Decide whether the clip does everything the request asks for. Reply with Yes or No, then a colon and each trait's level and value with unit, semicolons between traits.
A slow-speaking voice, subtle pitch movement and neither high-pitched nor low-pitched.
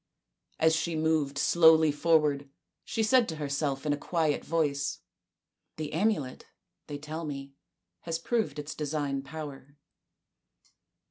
Yes: slow, 130 wpm; narrow, 2.3 semitones; medium, 150 Hz